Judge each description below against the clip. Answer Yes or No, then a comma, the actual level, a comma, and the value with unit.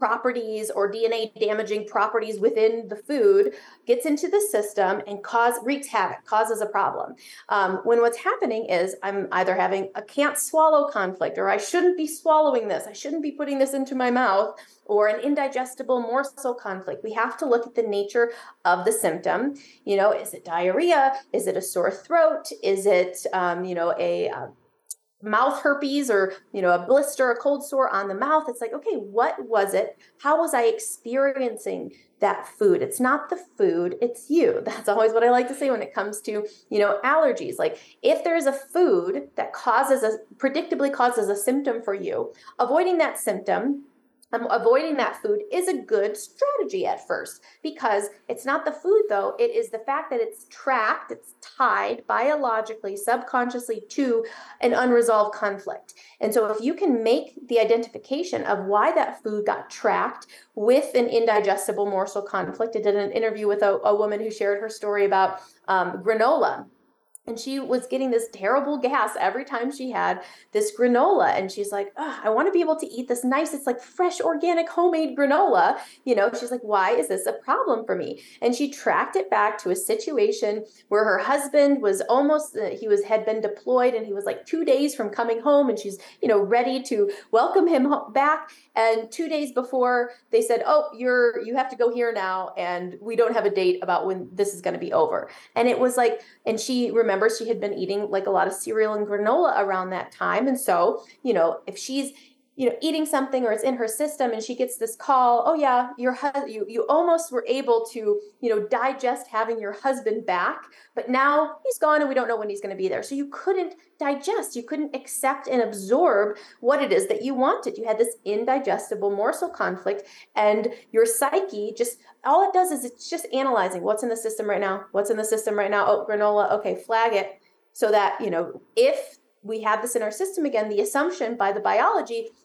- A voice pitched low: No, high, 245 Hz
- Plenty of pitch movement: Yes, wide, 5.8 semitones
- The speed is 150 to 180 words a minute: No, average, 200 wpm